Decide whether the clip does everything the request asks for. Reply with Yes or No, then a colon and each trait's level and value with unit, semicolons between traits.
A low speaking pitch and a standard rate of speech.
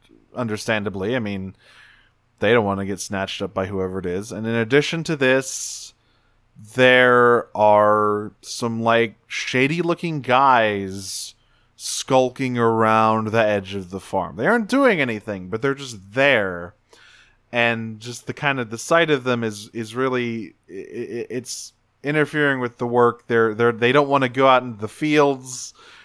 Yes: low, 120 Hz; average, 160 wpm